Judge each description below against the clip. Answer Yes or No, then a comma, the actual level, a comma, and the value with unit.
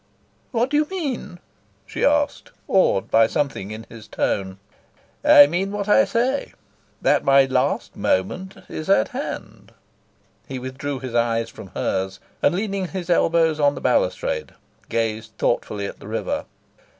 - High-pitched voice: No, medium, 150 Hz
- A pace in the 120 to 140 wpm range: No, average, 150 wpm